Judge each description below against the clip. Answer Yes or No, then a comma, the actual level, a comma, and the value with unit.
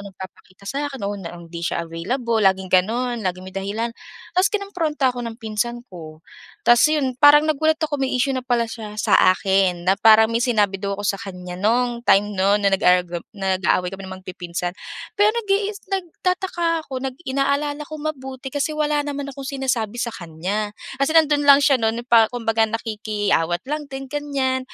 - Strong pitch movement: Yes, wide, 6.5 semitones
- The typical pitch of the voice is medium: No, high, 235 Hz